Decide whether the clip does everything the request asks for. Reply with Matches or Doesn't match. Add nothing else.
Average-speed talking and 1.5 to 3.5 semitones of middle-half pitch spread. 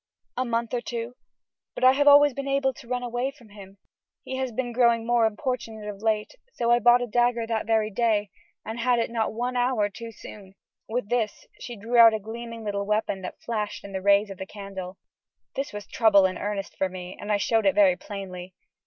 Doesn't match